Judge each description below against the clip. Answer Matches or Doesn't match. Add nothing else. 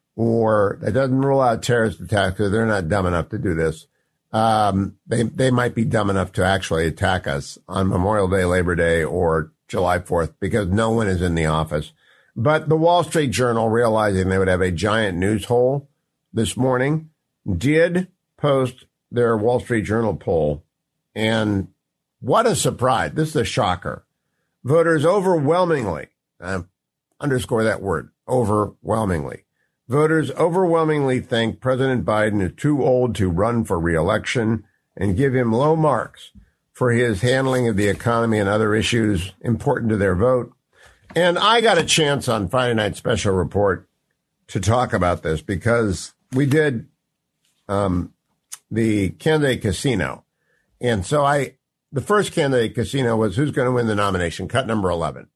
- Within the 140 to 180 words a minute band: Matches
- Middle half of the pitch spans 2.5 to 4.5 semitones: Doesn't match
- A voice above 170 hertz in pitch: Doesn't match